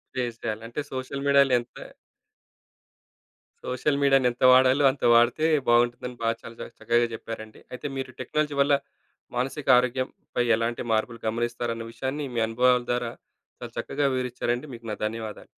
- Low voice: Yes, low, 125 Hz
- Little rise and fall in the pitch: Yes, narrow, 2.1 semitones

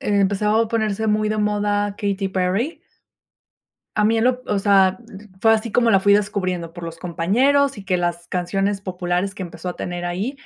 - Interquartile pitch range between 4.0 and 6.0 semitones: No, average, 2.9 semitones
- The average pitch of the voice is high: Yes, high, 200 Hz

